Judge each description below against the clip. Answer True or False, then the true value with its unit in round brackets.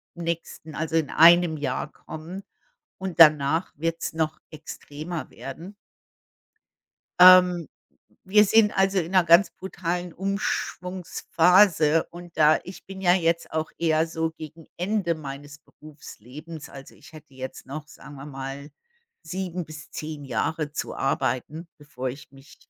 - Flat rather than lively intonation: False (3.2 semitones)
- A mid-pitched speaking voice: True (160 Hz)